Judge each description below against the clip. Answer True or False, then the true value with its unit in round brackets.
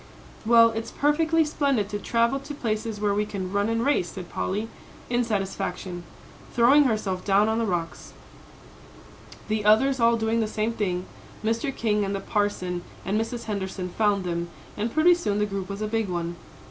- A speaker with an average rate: True (180 wpm)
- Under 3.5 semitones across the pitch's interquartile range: True (2.9 semitones)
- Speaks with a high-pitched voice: True (215 Hz)